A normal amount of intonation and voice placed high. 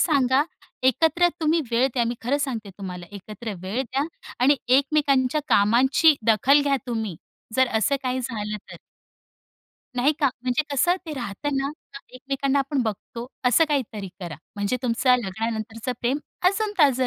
Yes: average, 4.0 semitones; very high, 255 Hz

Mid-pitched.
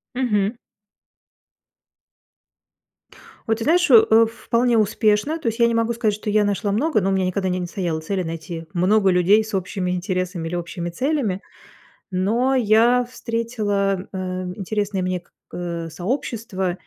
No: high, 205 Hz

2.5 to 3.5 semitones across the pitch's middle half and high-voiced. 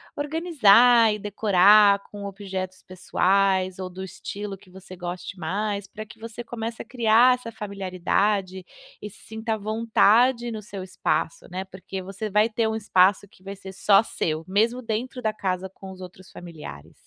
Yes: average, 2.9 semitones; high, 200 Hz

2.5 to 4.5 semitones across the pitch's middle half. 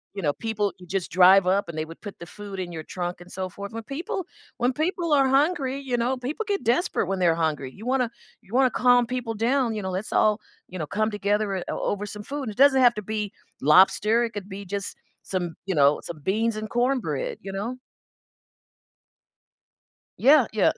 No: average, 5.1 semitones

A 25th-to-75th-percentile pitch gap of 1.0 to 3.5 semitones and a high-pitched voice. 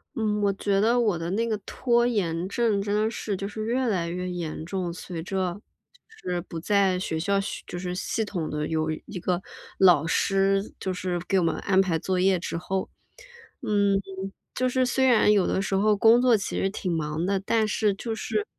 Yes: average, 3.2 semitones; high, 195 Hz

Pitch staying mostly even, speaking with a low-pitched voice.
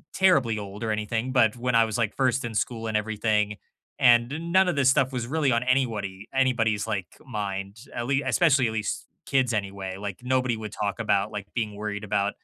No: average, 3.6 semitones; low, 115 Hz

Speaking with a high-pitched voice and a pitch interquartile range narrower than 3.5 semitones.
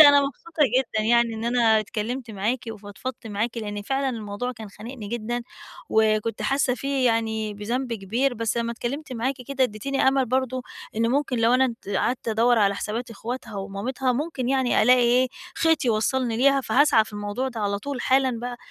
Yes: high, 240 Hz; average, 3.0 semitones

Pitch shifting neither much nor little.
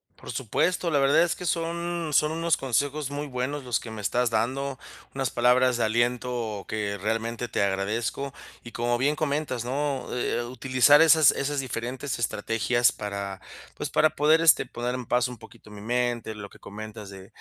Yes: average, 4.1 semitones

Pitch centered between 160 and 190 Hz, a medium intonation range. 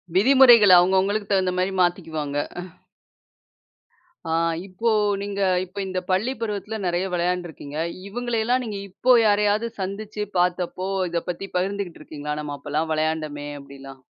Yes: medium, 185 Hz; average, 4.4 semitones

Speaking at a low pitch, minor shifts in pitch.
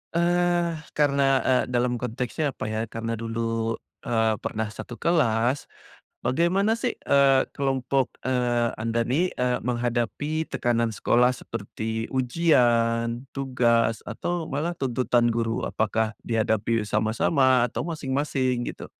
No: low, 125 Hz; average, 3.2 semitones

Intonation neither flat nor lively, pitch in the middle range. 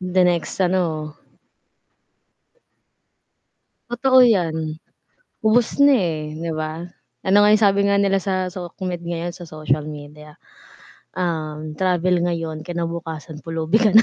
Yes: average, 3.3 semitones; medium, 175 Hz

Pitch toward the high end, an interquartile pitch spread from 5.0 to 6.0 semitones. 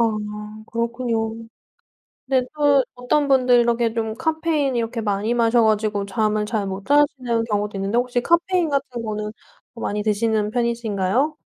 No: high, 230 Hz; average, 3.2 semitones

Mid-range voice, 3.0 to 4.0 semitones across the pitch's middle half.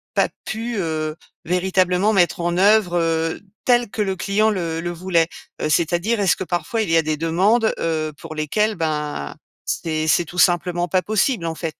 Yes: medium, 175 Hz; average, 3.4 semitones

